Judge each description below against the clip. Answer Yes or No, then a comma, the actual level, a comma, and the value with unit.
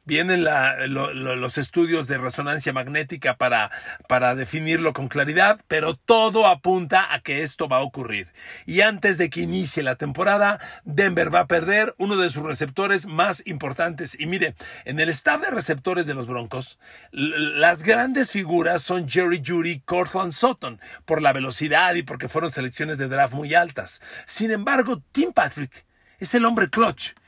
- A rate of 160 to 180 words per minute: Yes, average, 170 wpm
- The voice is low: No, medium, 170 Hz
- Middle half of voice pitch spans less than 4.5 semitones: No, average, 4.9 semitones